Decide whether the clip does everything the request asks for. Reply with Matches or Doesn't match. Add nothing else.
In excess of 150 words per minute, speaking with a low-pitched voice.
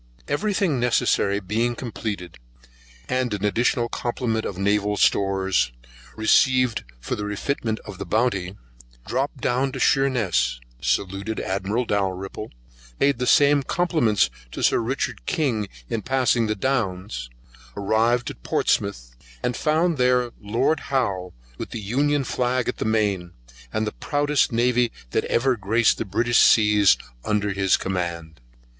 Doesn't match